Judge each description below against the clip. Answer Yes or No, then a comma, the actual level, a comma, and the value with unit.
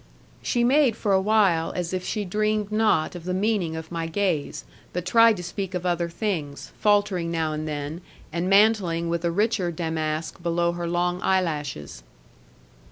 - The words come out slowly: No, average, 165 wpm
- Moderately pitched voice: Yes, medium, 180 Hz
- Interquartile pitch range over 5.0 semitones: No, average, 3.7 semitones